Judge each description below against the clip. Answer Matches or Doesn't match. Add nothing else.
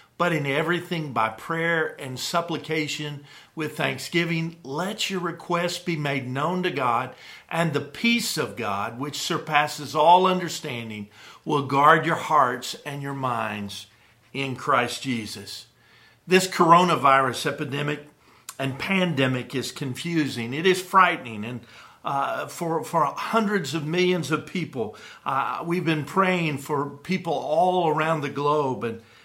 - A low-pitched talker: Doesn't match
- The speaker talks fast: Doesn't match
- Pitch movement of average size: Matches